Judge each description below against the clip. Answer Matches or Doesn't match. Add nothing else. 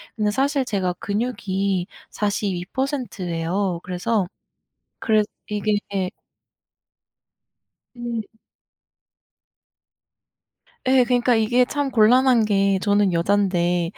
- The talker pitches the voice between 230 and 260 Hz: Doesn't match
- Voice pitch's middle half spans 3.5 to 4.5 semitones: Matches